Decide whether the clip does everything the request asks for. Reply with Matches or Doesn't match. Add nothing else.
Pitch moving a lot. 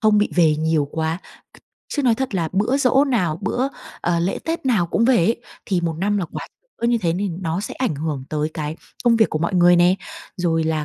Matches